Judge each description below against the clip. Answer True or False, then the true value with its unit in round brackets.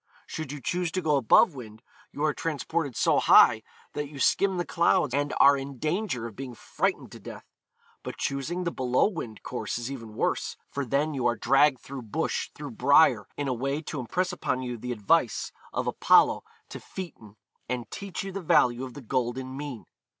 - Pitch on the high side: False (135 Hz)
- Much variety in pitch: False (4.2 semitones)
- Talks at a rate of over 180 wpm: True (195 wpm)